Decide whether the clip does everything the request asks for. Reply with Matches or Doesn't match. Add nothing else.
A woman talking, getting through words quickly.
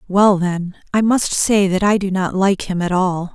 Matches